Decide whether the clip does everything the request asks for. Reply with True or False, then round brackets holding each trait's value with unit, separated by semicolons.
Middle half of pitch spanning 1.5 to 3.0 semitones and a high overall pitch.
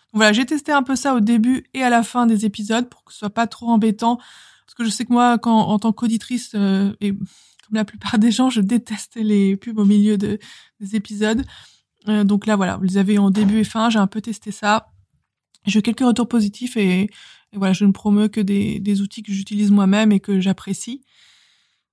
True (2.4 semitones; 215 Hz)